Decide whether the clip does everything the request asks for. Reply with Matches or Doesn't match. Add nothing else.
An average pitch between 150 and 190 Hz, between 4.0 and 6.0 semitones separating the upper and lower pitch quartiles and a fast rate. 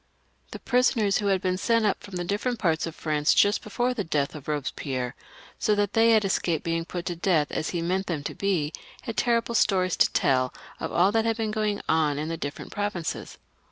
Matches